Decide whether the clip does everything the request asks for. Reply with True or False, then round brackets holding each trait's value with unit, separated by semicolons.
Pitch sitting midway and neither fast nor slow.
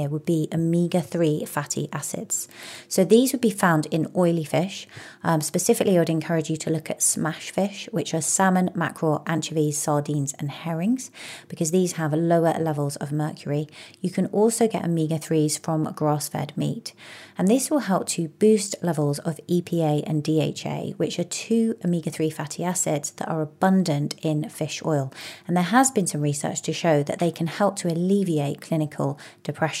True (165 Hz; 180 wpm)